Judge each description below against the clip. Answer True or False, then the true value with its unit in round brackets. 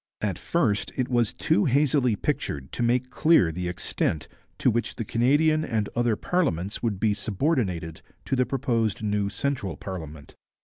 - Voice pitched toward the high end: False (115 Hz)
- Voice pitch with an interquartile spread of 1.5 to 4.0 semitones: False (5.1 semitones)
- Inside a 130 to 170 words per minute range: True (160 wpm)